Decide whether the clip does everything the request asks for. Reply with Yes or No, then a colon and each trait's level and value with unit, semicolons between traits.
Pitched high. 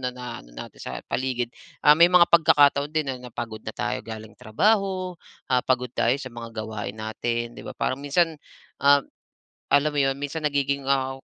No: low, 135 Hz